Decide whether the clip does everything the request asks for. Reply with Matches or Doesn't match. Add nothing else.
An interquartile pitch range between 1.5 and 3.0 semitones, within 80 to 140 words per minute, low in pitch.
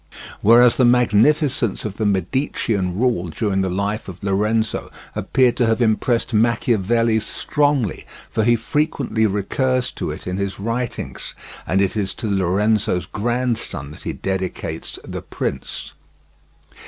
Doesn't match